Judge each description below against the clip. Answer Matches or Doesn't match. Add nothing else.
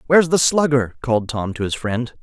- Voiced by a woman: Doesn't match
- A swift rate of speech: Matches